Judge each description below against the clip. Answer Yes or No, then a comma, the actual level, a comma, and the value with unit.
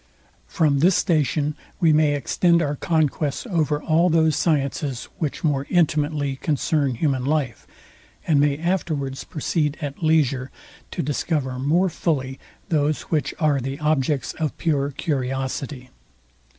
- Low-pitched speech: No, medium, 150 Hz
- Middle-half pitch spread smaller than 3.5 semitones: Yes, narrow, 2.6 semitones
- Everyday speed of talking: No, slow, 130 wpm